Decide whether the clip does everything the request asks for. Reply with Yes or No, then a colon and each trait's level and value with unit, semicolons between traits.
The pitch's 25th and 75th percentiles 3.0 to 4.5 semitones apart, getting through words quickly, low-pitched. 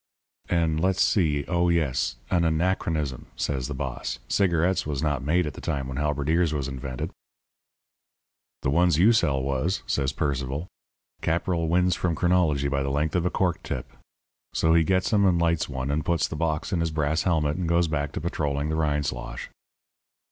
No: average, 3.4 semitones; average, 185 wpm; very low, 80 Hz